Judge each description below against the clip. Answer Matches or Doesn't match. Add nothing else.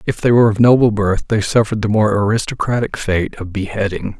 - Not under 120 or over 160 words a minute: Doesn't match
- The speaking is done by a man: Matches